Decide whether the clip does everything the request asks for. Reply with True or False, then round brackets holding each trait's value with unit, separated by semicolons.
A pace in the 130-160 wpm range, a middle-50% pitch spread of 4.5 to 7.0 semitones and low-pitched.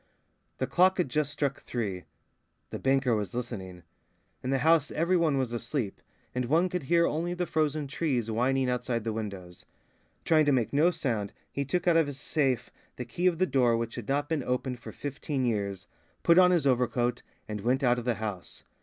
False (200 wpm; 5.1 semitones; 130 Hz)